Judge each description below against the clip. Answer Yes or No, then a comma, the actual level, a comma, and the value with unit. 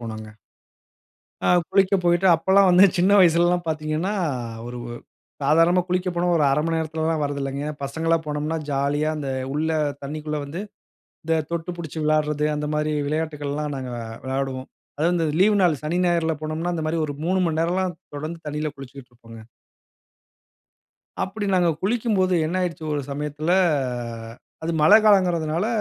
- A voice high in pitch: No, medium, 160 Hz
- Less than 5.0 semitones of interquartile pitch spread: Yes, average, 3.0 semitones